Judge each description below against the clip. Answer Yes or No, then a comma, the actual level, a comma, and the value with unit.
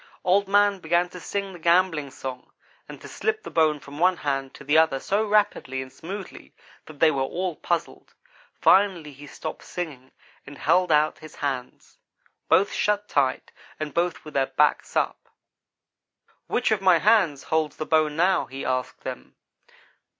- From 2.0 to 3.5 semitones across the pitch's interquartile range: No, average, 4.8 semitones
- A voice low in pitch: No, medium, 160 Hz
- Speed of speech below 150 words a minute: No, average, 170 wpm